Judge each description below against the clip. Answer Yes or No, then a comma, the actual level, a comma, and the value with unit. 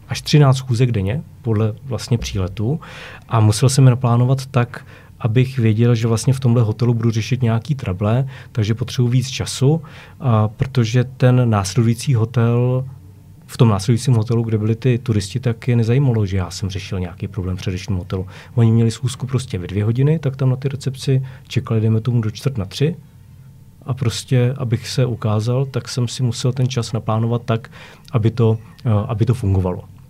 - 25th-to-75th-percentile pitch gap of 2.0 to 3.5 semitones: Yes, average, 2.7 semitones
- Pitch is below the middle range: Yes, low, 120 Hz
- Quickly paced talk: Yes, fast, 175 wpm